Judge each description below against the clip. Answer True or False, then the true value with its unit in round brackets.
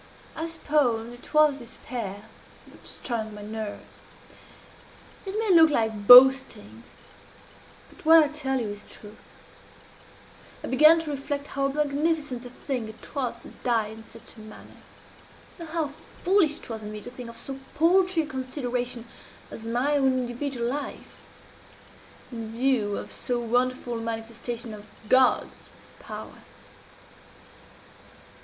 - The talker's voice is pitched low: False (250 Hz)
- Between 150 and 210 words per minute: False (140 wpm)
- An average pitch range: True (4.4 semitones)